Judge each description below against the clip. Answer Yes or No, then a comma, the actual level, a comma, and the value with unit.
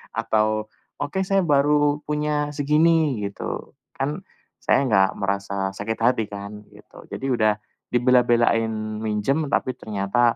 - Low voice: Yes, low, 120 Hz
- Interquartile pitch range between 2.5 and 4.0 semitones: No, wide, 5.6 semitones